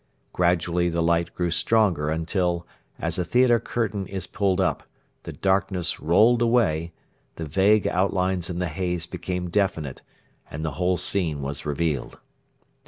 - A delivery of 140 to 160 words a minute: Yes, average, 145 wpm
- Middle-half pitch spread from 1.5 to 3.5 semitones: Yes, average, 2.7 semitones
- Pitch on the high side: No, very low, 90 Hz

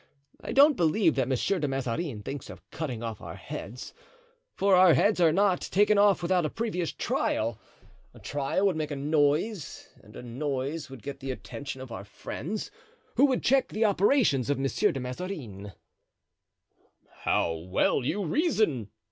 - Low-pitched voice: No, medium, 150 Hz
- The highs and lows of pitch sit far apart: Yes, wide, 7.3 semitones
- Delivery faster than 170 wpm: No, average, 160 wpm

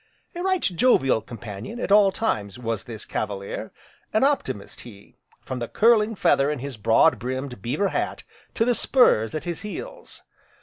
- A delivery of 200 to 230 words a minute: No, average, 165 wpm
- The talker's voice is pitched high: No, medium, 140 Hz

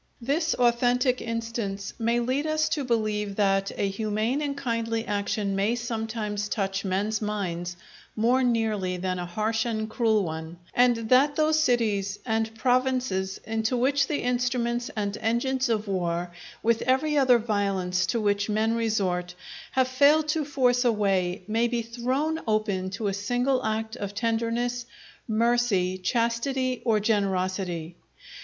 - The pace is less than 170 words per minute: Yes, average, 145 wpm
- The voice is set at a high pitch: Yes, high, 225 Hz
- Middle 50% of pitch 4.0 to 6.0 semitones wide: No, average, 3.5 semitones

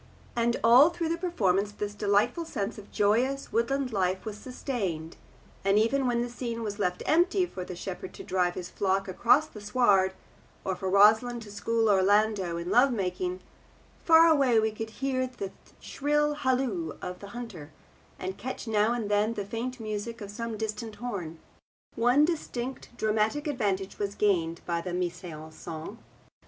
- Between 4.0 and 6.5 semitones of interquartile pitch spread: Yes, average, 4.4 semitones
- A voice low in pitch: No, high, 215 Hz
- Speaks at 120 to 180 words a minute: Yes, average, 170 wpm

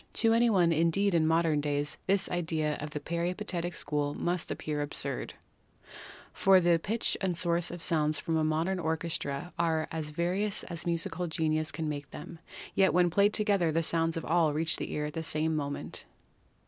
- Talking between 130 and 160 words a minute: No, average, 185 wpm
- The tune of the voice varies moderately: No, narrow, 2.3 semitones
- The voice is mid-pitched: Yes, medium, 165 Hz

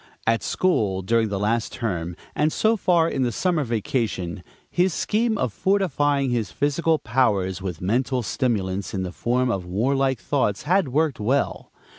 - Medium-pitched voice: No, low, 125 Hz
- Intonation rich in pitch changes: Yes, wide, 6.4 semitones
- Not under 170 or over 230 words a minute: No, average, 160 wpm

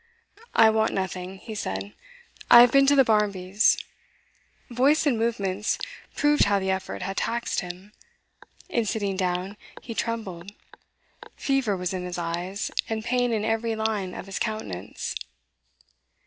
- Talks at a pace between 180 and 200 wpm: No, average, 140 wpm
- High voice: Yes, high, 210 Hz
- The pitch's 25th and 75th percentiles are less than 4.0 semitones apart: Yes, average, 3.6 semitones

